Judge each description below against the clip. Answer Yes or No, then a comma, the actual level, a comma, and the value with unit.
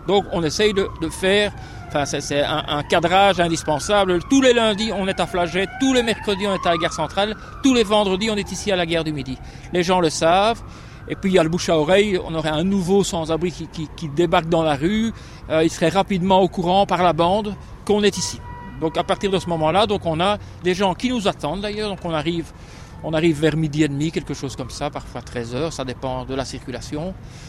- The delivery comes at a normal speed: No, fast, 245 wpm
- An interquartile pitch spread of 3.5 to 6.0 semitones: Yes, average, 4.2 semitones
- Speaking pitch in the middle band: Yes, medium, 175 Hz